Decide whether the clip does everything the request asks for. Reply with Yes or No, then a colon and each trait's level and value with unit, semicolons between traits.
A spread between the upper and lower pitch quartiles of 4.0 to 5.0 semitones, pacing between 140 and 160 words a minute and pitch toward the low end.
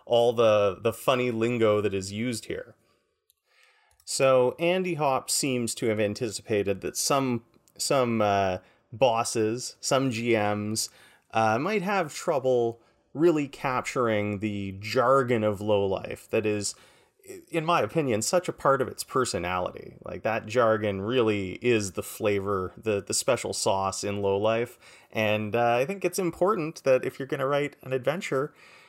Yes: average, 4.4 semitones; average, 150 wpm; low, 115 Hz